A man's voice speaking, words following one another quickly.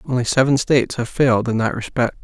Yes: male; fast, 215 wpm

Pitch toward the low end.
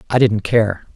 Yes: low, 110 Hz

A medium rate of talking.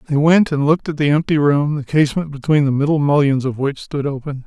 No: fast, 240 wpm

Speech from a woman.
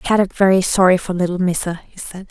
Yes: female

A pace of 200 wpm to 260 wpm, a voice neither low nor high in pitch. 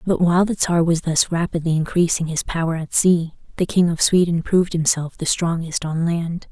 Yes: fast, 205 wpm; medium, 170 Hz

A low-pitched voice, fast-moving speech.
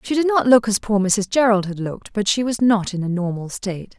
No: high, 210 Hz; fast, 270 wpm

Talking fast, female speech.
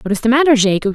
Yes: fast, 320 wpm; female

